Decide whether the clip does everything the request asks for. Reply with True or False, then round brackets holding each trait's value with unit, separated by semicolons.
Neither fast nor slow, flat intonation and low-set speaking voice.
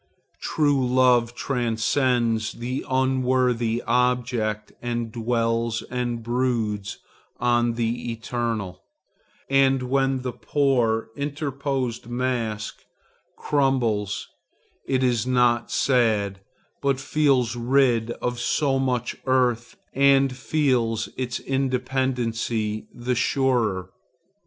False (90 wpm; 2.3 semitones; 125 Hz)